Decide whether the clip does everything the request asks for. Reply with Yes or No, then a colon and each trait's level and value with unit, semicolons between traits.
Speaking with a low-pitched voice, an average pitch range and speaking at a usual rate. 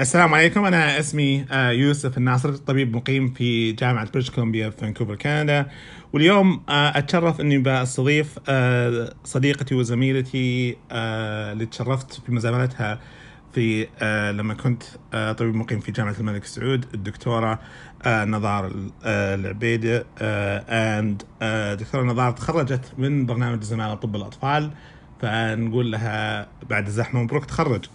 No: low, 125 Hz; average, 3.7 semitones; slow, 110 wpm